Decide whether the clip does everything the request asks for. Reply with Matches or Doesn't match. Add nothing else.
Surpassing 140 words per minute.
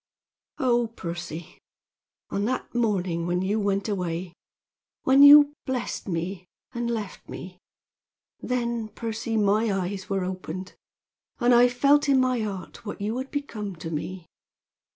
Doesn't match